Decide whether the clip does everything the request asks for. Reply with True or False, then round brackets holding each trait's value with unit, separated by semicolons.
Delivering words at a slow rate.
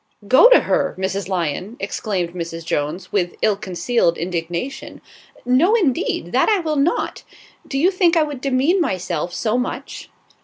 False (155 wpm)